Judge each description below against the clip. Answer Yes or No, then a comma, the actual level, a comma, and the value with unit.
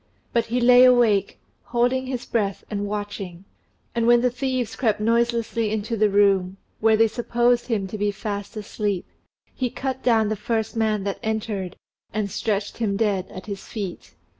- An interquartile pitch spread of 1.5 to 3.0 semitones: Yes, average, 2.7 semitones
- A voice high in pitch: Yes, high, 220 Hz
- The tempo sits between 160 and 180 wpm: Yes, average, 170 wpm